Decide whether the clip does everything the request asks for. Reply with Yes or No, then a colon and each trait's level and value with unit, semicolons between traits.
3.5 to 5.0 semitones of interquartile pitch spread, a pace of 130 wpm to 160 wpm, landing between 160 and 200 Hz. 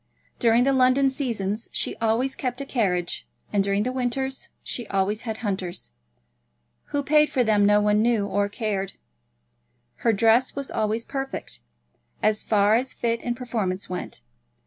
No: average, 3.9 semitones; average, 155 wpm; high, 225 Hz